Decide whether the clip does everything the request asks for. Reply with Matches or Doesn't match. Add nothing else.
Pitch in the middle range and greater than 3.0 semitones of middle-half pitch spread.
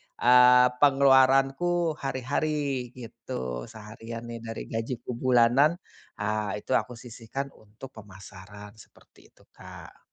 Doesn't match